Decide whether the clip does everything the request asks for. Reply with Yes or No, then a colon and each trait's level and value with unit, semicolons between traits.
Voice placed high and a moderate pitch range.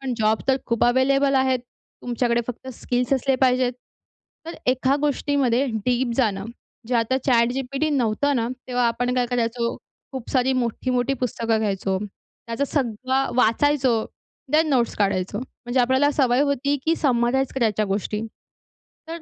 No: very high, 250 Hz; narrow, 2.3 semitones